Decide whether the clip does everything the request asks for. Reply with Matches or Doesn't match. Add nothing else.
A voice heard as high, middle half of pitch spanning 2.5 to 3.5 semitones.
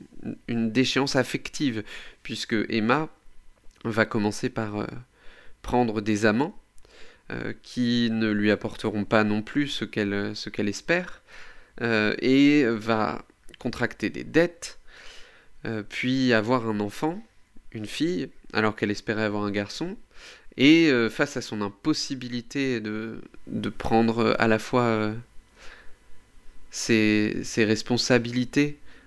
Doesn't match